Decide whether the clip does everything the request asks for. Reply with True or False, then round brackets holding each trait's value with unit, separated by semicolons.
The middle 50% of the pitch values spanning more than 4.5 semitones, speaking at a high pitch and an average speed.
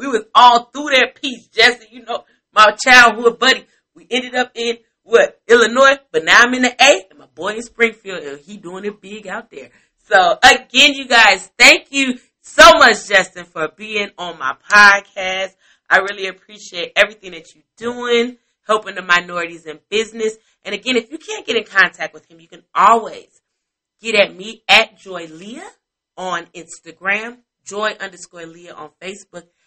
True (4.9 semitones; 215 Hz; 180 wpm)